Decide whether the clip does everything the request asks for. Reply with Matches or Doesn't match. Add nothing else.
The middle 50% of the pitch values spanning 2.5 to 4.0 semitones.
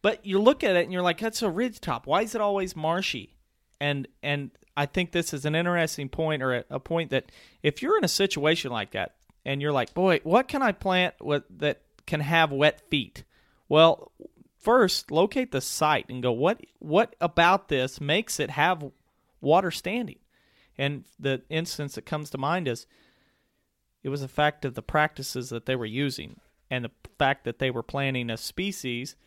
Doesn't match